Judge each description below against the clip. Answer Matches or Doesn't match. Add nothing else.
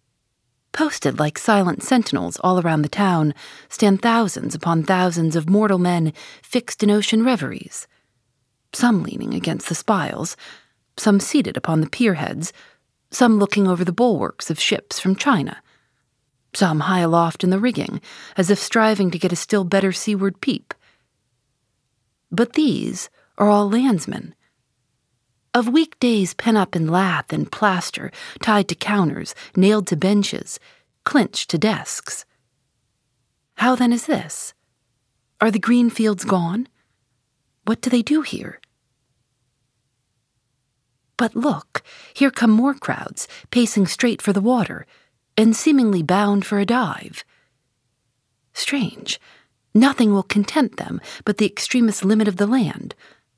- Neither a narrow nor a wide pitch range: Doesn't match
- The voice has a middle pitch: Doesn't match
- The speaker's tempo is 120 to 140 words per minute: Matches